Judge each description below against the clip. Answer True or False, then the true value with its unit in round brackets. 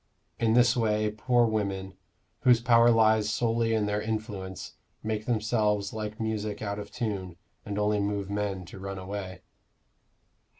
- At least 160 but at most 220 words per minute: False (145 wpm)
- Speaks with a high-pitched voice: False (105 Hz)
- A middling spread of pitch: False (1.8 semitones)